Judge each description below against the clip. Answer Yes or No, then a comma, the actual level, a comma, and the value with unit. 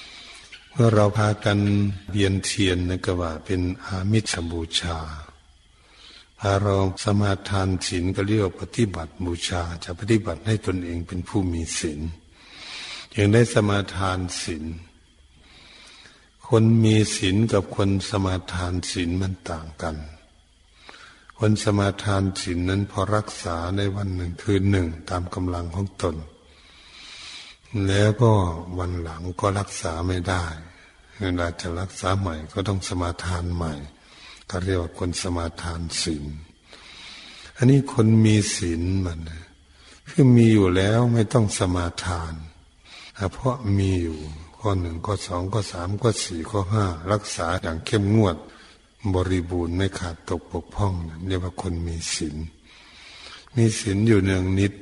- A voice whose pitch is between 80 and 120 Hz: Yes, very low, 90 Hz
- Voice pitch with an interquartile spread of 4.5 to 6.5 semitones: No, average, 3.1 semitones